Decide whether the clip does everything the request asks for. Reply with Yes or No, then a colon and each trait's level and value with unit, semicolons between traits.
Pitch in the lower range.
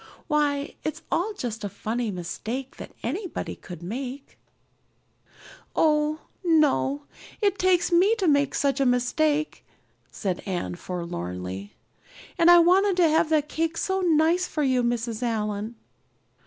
No: very high, 285 Hz